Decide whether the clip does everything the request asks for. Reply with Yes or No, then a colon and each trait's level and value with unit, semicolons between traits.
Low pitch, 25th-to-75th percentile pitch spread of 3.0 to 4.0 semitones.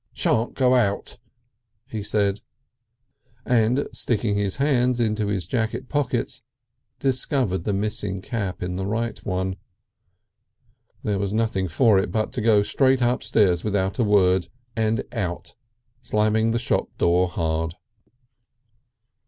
Yes: low, 105 Hz; average, 3.5 semitones